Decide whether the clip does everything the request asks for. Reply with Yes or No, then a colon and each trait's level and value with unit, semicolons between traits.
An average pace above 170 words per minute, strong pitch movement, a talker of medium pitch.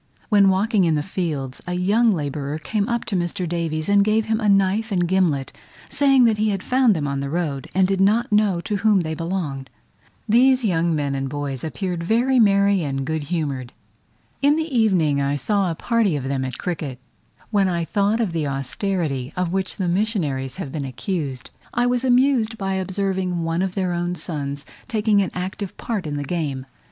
Yes: average, 200 wpm; wide, 5.8 semitones; medium, 180 Hz